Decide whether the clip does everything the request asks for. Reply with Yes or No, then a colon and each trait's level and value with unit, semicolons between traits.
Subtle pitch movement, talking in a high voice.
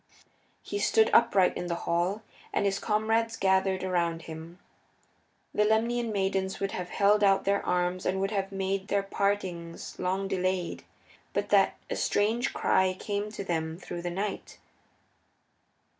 Yes: narrow, 2.3 semitones; high, 195 Hz